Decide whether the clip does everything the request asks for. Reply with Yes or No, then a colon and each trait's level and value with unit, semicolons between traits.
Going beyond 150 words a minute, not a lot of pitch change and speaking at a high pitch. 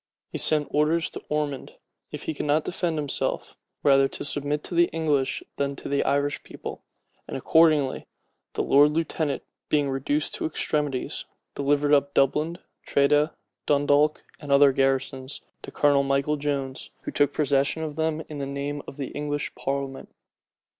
No: average, 160 wpm; narrow, 1.5 semitones; medium, 145 Hz